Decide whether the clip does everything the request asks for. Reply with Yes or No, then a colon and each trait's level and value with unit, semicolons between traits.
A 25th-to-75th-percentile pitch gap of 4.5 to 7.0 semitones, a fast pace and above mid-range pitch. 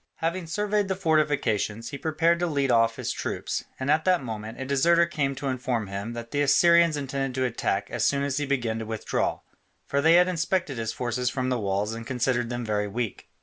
No: wide, 5.5 semitones; fast, 215 wpm; low, 135 Hz